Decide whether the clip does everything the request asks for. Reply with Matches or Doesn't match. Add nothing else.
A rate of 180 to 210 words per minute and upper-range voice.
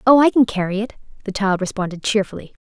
Matches